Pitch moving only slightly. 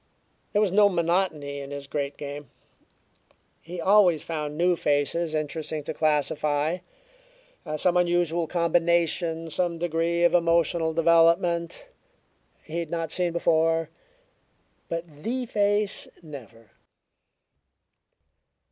Yes: narrow, 2.2 semitones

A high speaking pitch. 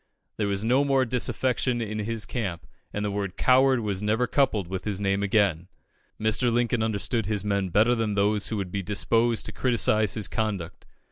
No: low, 105 Hz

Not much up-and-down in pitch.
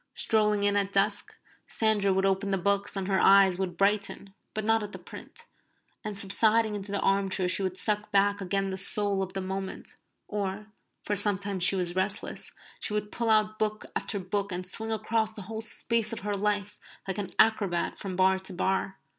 Yes: narrow, 1.7 semitones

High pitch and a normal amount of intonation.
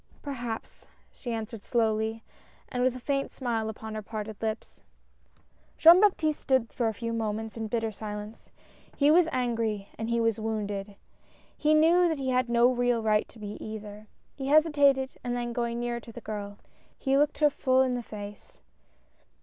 Yes: high, 235 Hz; average, 3.3 semitones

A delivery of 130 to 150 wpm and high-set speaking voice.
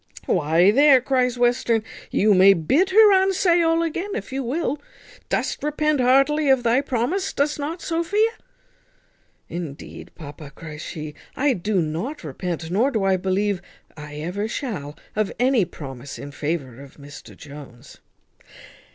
Yes: average, 145 wpm; high, 220 Hz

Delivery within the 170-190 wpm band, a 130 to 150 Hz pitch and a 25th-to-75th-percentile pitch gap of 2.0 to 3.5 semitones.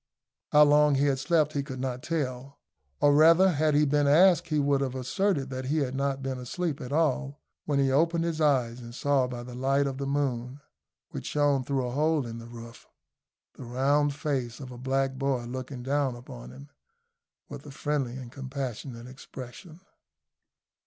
Yes: average, 185 wpm; low, 135 Hz; narrow, 2.5 semitones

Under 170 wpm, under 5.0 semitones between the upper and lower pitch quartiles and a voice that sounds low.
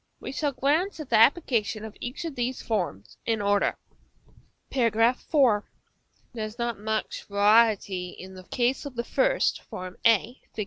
No: average, 160 wpm; average, 3.9 semitones; high, 230 Hz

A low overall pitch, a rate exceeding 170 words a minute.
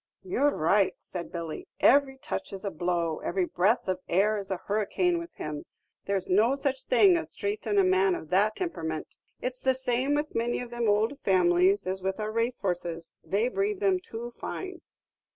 No: high, 220 Hz; average, 190 wpm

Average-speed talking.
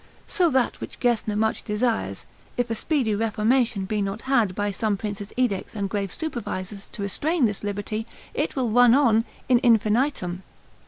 Yes: average, 165 wpm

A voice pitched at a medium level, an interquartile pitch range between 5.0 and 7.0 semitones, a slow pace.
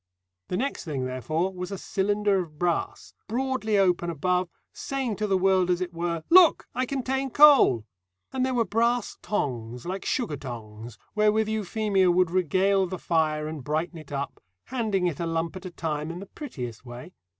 No: medium, 180 Hz; wide, 5.5 semitones; average, 180 wpm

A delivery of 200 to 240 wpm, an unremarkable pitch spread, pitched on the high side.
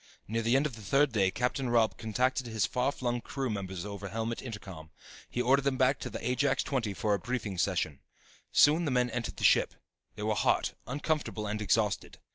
No: fast, 205 wpm; average, 3.8 semitones; low, 115 Hz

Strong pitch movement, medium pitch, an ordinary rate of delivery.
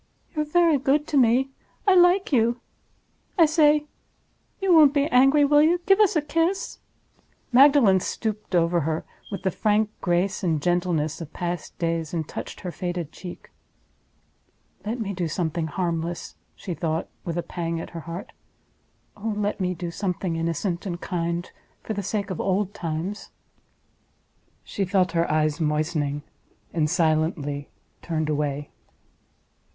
Yes: wide, 6.9 semitones; medium, 180 Hz; average, 145 wpm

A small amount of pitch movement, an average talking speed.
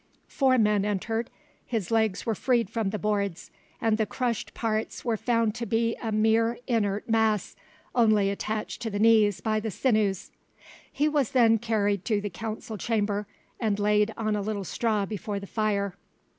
Yes: narrow, 1.8 semitones; average, 170 wpm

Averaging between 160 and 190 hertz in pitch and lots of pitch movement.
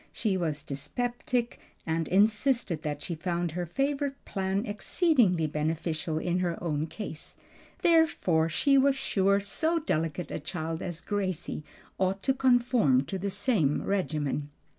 Yes: medium, 185 Hz; wide, 6.9 semitones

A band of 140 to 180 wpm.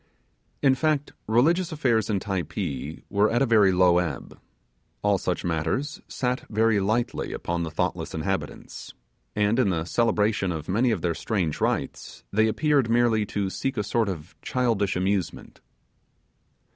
Yes: average, 150 wpm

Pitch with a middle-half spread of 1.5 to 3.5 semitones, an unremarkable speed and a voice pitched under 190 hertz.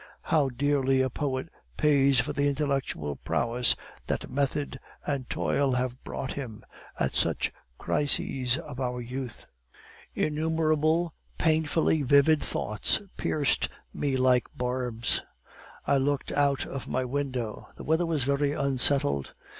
No: narrow, 2.4 semitones; slow, 125 wpm; low, 135 Hz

